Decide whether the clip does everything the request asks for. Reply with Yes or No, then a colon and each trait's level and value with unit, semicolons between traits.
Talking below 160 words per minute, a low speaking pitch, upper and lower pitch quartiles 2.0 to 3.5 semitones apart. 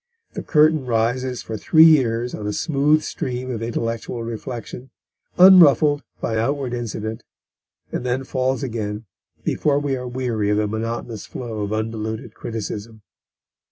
Yes: average, 140 wpm; low, 120 Hz; average, 3.2 semitones